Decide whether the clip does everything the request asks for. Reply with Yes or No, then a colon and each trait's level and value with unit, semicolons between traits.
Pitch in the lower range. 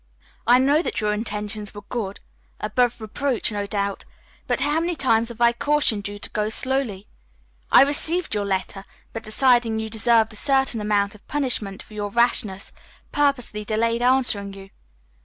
No: high, 225 Hz